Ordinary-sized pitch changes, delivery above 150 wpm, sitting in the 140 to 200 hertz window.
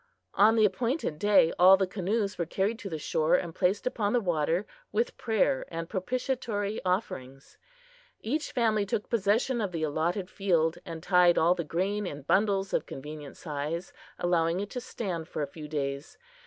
Yes: average, 4.4 semitones; average, 175 wpm; medium, 185 Hz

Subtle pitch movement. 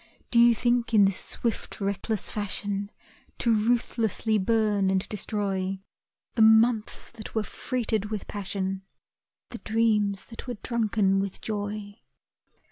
Yes: narrow, 2.3 semitones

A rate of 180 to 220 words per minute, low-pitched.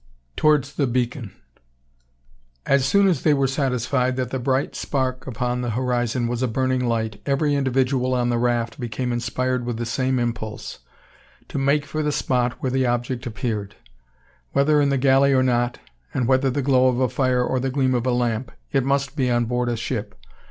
Yes: average, 195 wpm; low, 130 Hz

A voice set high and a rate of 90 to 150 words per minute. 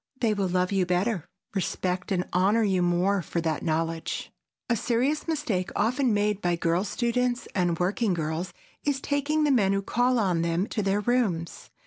No: high, 195 Hz; average, 175 wpm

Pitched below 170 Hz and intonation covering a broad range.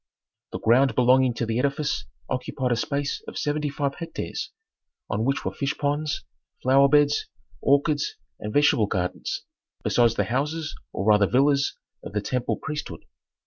No: medium, 140 Hz; average, 3.4 semitones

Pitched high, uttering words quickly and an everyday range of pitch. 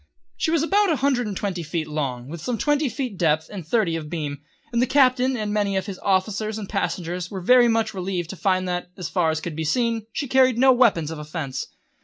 No: high, 195 Hz; fast, 240 wpm; wide, 6.7 semitones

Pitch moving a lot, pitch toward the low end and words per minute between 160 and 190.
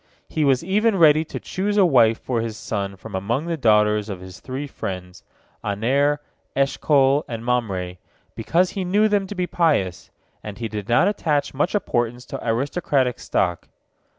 Yes: wide, 7.4 semitones; low, 130 Hz; average, 170 wpm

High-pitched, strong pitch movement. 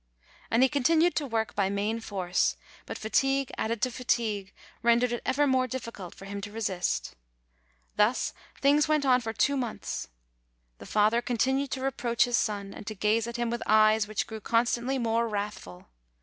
No: high, 230 Hz; average, 3.4 semitones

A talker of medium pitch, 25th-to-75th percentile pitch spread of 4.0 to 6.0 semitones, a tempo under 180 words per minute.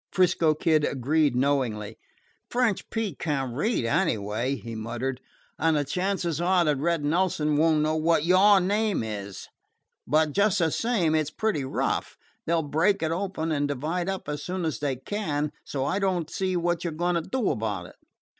No: medium, 160 Hz; average, 4.4 semitones; average, 185 wpm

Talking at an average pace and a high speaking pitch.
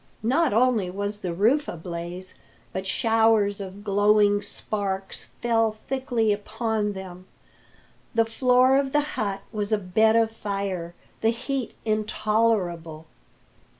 No: slow, 120 wpm; high, 210 Hz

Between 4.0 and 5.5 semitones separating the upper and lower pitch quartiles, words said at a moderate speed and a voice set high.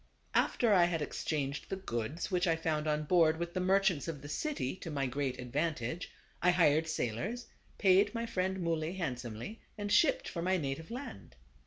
No: average, 4.7 semitones; average, 190 wpm; medium, 165 Hz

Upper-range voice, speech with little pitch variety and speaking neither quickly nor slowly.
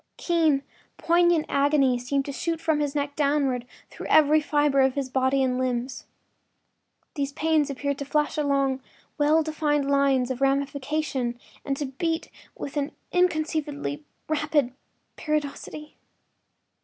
No: very high, 285 Hz; narrow, 2.0 semitones; slow, 130 wpm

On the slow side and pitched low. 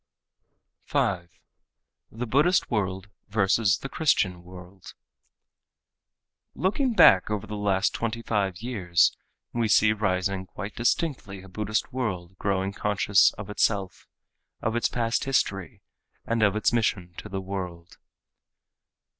Yes: slow, 120 wpm; low, 100 Hz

